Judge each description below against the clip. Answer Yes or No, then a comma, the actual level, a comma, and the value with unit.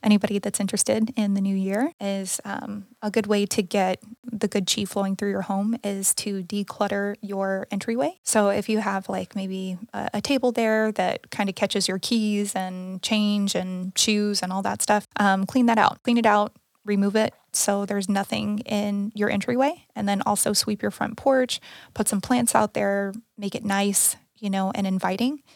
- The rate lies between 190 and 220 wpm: Yes, average, 195 wpm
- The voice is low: No, high, 205 Hz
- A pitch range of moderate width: No, narrow, 1.7 semitones